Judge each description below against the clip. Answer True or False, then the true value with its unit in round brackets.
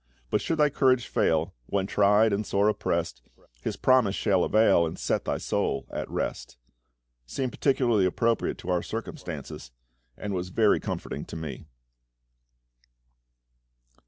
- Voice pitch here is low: True (100 Hz)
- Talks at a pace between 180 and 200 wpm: False (135 wpm)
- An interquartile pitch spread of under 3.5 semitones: False (4.8 semitones)